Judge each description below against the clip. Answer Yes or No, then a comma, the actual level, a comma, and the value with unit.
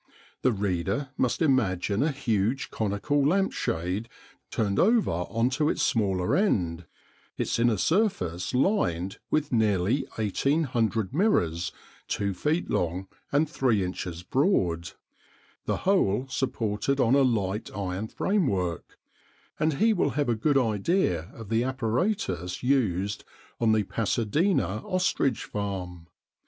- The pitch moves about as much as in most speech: No, wide, 6.8 semitones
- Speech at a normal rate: No, slow, 125 wpm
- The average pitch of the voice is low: Yes, low, 115 Hz